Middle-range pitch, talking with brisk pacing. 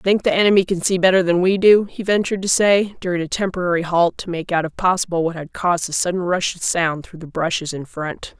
Yes: medium, 180 Hz; fast, 245 wpm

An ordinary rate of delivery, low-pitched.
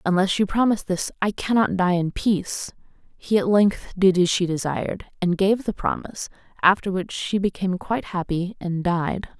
No: average, 180 wpm; high, 190 Hz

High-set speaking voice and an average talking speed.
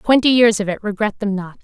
No: high, 210 Hz; fast, 255 wpm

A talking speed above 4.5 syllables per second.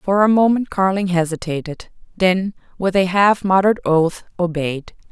Yes: 4.7 syllables/s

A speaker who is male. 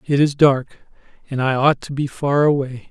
Yes: male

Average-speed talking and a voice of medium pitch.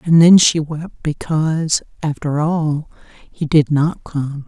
Yes: average, 150 wpm; medium, 155 Hz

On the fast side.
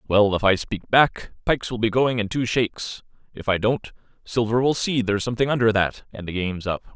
Yes: fast, 225 wpm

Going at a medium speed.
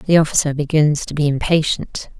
Yes: average, 165 wpm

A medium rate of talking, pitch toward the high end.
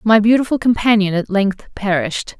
Yes: average, 150 wpm; high, 210 Hz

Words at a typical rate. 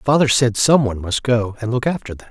No: fast, 260 wpm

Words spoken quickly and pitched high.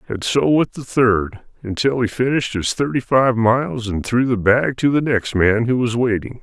No: fast, 215 wpm; low, 120 Hz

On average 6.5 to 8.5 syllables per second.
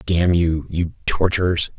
No: 4.0 syllables/s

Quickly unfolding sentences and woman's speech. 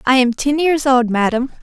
Yes: fast, 220 wpm; female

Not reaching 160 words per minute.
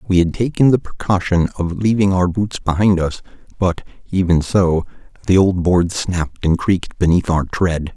No: average, 175 wpm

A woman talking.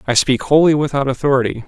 No: male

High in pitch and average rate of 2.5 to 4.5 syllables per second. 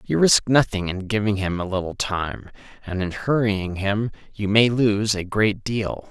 No: low, 105 Hz; 4.2 syllables/s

